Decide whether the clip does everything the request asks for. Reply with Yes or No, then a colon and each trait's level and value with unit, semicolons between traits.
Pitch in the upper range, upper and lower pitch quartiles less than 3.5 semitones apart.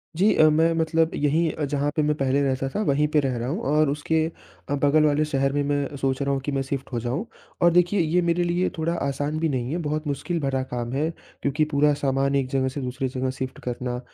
No: medium, 145 Hz; average, 2.7 semitones